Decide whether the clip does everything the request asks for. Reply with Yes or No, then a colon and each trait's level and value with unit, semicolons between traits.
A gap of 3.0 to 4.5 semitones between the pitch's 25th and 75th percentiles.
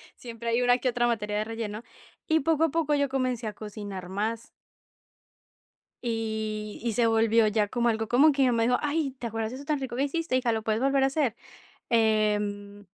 Yes: average, 3.5 semitones